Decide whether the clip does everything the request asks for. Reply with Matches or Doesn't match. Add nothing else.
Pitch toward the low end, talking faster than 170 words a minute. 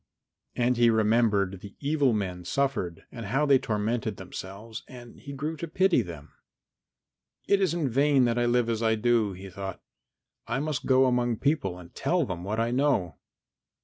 Matches